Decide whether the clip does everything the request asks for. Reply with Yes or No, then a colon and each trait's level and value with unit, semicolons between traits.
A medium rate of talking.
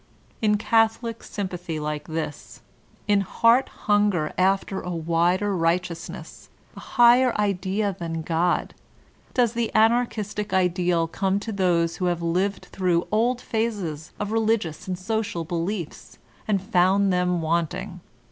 No: slow, 130 wpm